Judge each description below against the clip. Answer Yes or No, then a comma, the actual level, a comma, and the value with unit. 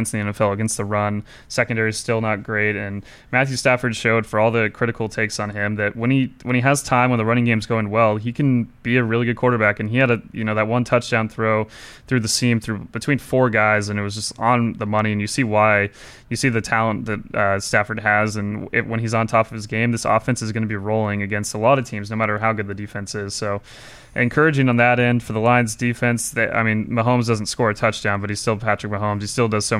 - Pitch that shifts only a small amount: Yes, narrow, 2.3 semitones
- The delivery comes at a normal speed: No, fast, 270 wpm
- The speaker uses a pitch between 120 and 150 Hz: No, low, 110 Hz